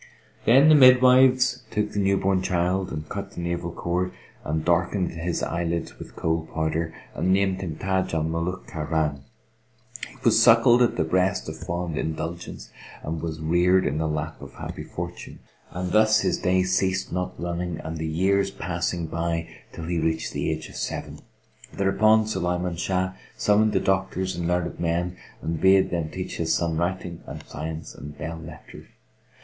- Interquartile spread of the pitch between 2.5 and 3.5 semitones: Yes, average, 2.9 semitones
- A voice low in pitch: Yes, very low, 90 Hz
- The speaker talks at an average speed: Yes, average, 170 wpm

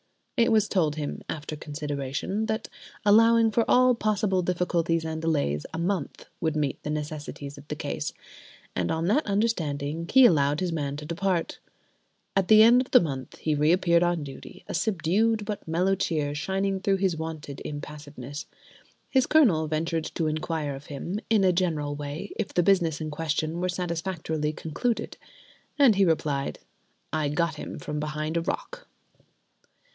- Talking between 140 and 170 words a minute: Yes, average, 165 wpm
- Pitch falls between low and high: Yes, medium, 165 Hz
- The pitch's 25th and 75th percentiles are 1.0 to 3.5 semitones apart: No, average, 4.5 semitones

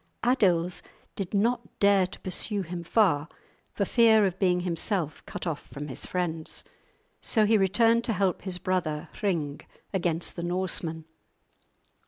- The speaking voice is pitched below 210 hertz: Yes, medium, 185 Hz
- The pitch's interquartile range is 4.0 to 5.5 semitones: No, average, 3.3 semitones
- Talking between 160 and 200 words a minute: No, average, 145 wpm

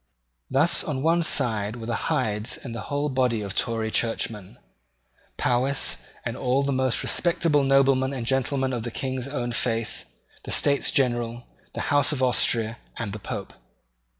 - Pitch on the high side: No, low, 130 Hz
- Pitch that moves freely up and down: No, average, 3.1 semitones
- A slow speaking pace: No, average, 160 wpm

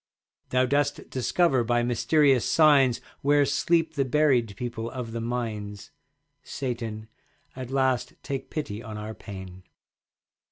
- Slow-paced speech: Yes, slow, 125 wpm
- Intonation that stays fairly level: No, average, 3.7 semitones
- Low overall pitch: Yes, low, 125 Hz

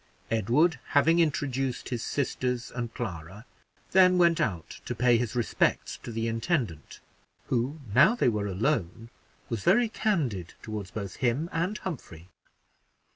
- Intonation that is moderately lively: No, wide, 6.5 semitones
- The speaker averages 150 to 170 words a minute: No, slow, 135 wpm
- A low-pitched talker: Yes, low, 125 Hz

